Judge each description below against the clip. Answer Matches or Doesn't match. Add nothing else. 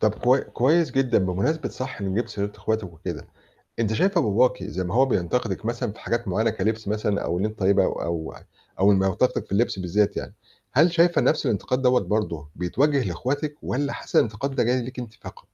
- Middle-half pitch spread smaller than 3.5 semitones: Doesn't match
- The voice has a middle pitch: Doesn't match